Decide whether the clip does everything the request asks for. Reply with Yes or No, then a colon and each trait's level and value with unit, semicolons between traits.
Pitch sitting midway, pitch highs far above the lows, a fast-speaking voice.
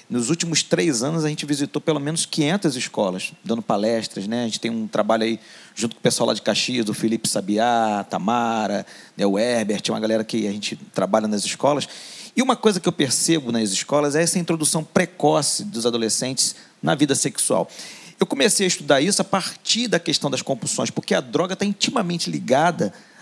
Yes: medium, 145 Hz; wide, 6.9 semitones; fast, 195 wpm